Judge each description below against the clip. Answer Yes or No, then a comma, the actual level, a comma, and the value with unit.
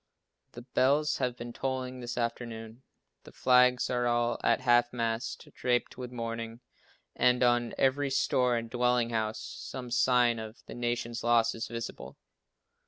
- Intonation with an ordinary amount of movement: No, narrow, 1.3 semitones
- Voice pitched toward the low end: Yes, low, 120 Hz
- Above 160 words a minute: No, average, 150 wpm